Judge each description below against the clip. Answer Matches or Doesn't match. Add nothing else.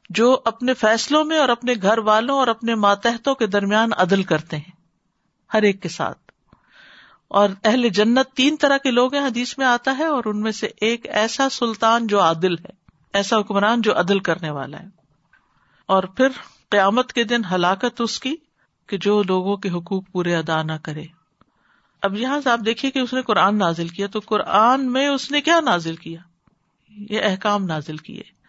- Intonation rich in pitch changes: Doesn't match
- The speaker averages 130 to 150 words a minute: Doesn't match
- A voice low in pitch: Doesn't match